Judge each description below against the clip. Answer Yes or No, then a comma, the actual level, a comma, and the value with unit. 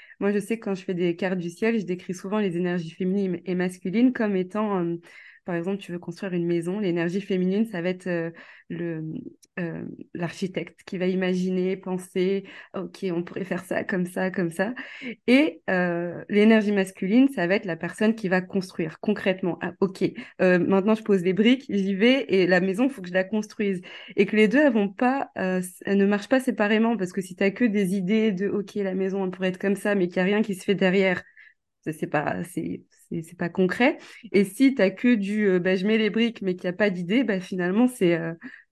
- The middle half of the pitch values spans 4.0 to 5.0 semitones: No, narrow, 2.6 semitones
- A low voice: No, high, 190 Hz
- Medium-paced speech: No, fast, 235 wpm